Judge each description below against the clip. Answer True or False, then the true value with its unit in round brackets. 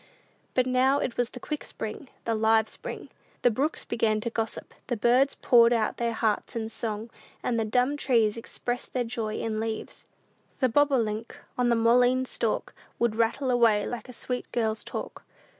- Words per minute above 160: True (175 wpm)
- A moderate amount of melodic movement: False (2.1 semitones)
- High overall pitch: True (235 Hz)